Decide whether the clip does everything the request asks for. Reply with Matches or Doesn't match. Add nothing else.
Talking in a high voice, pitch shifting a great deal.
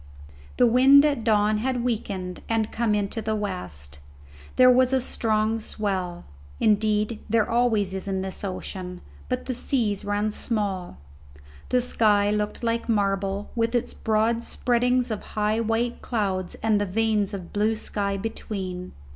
Doesn't match